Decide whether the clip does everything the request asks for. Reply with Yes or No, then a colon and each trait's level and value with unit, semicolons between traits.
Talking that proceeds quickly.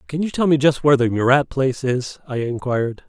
Yes: fast, 235 wpm